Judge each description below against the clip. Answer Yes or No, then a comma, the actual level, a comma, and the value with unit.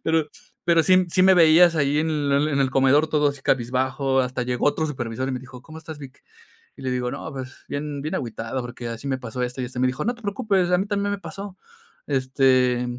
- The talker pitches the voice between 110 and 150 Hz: Yes, medium, 140 Hz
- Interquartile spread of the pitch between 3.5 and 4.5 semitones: Yes, average, 4.0 semitones